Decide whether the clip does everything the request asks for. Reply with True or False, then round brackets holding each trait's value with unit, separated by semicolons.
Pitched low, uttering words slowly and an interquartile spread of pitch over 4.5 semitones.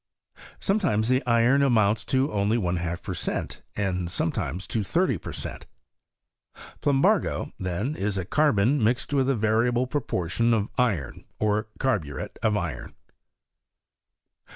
True (110 Hz; 130 wpm; 5.0 semitones)